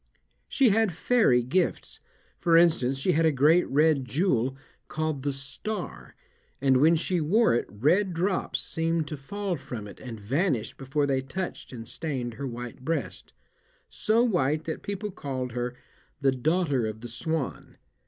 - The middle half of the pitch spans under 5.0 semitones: No, average, 5.3 semitones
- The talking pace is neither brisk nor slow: Yes, average, 160 wpm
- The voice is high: No, medium, 150 Hz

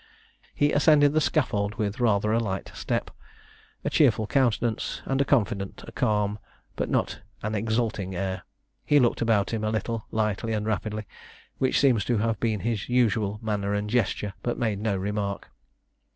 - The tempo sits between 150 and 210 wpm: Yes, average, 165 wpm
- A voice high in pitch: No, low, 110 Hz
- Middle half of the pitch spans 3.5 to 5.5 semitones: No, narrow, 2.5 semitones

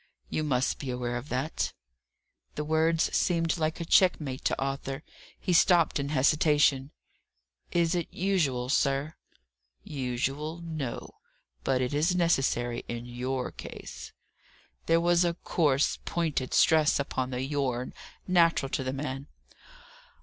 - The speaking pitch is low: No, medium, 145 Hz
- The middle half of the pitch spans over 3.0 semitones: Yes, average, 4.1 semitones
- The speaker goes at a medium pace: No, slow, 130 wpm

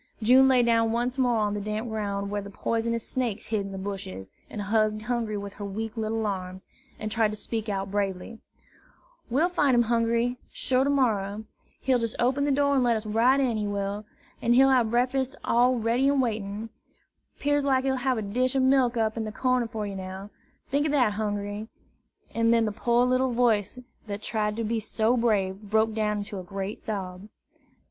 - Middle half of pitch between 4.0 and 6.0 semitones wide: No, average, 3.3 semitones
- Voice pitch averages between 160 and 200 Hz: No, high, 225 Hz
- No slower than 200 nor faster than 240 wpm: Yes, fast, 205 wpm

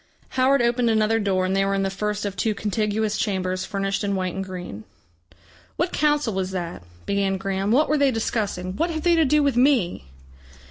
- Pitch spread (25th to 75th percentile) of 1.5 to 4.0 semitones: No, average, 4.4 semitones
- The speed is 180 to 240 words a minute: Yes, average, 200 wpm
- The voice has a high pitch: Yes, high, 205 Hz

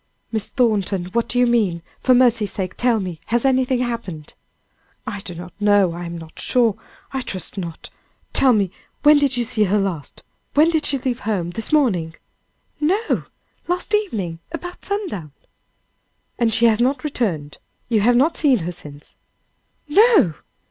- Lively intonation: Yes, wide, 6.4 semitones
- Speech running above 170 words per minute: No, average, 165 wpm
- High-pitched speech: Yes, high, 225 Hz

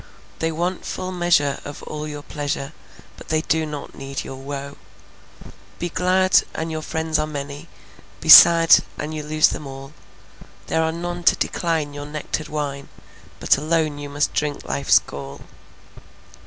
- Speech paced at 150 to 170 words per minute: Yes, average, 160 wpm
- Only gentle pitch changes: Yes, narrow, 2.2 semitones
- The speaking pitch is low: No, medium, 150 Hz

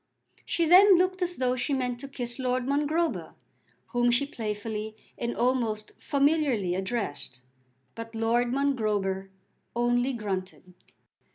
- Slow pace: Yes, slow, 120 wpm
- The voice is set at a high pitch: Yes, high, 245 Hz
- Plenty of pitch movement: No, average, 4.5 semitones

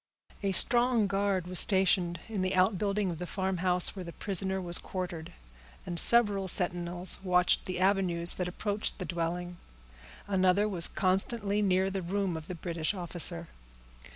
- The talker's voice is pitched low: No, medium, 185 Hz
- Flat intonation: Yes, narrow, 2.0 semitones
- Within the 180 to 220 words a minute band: No, average, 155 wpm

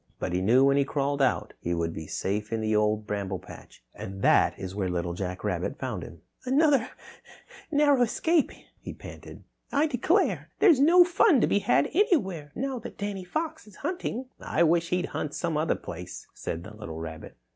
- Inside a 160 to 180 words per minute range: No, average, 190 wpm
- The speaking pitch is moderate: Yes, medium, 150 Hz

